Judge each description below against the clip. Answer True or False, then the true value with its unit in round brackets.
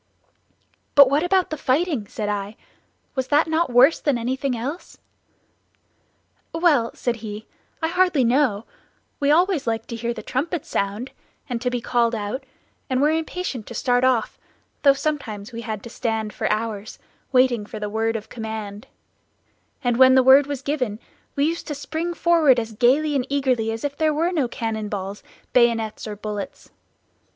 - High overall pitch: True (250 Hz)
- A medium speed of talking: True (170 wpm)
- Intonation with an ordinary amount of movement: True (4.6 semitones)